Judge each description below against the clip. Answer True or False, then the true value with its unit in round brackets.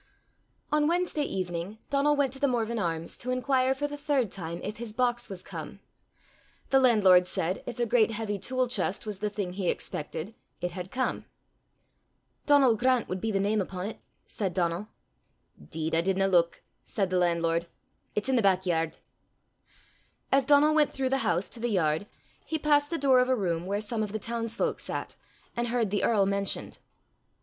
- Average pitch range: False (5.7 semitones)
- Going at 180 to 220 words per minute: True (190 wpm)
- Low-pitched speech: False (215 Hz)